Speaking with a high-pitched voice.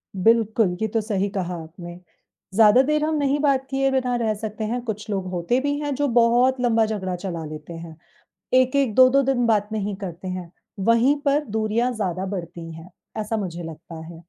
Yes: high, 215 Hz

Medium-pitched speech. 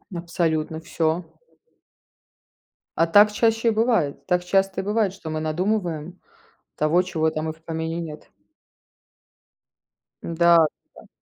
Yes: medium, 170 Hz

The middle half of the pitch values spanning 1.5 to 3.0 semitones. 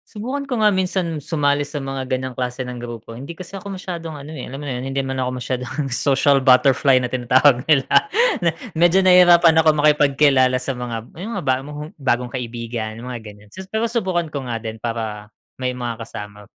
No: average, 4.7 semitones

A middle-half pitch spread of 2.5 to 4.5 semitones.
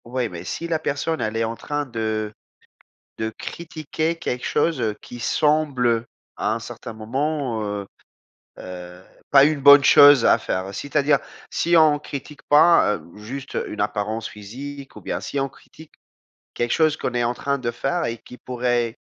No: average, 4.9 semitones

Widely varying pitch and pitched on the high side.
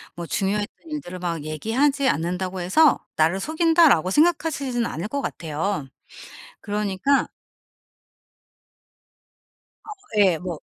Yes: wide, 8.2 semitones; high, 200 Hz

